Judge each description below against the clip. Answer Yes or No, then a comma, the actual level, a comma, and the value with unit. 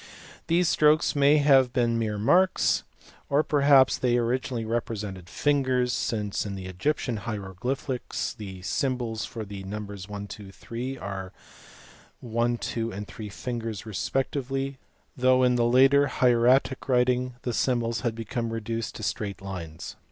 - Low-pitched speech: Yes, low, 120 Hz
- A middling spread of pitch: Yes, average, 3.8 semitones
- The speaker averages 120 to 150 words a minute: Yes, average, 140 wpm